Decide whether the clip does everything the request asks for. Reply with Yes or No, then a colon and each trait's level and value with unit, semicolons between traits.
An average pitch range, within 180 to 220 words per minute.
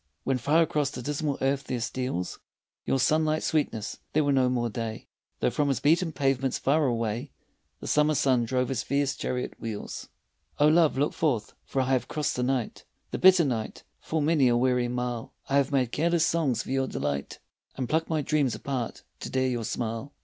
Yes: average, 3.4 semitones; average, 200 wpm